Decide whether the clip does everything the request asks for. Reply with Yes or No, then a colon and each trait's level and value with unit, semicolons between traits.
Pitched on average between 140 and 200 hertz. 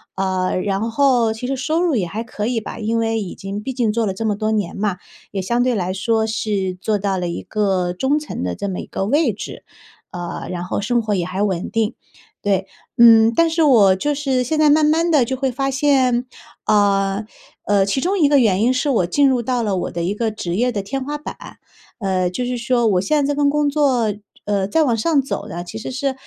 No: high, 225 Hz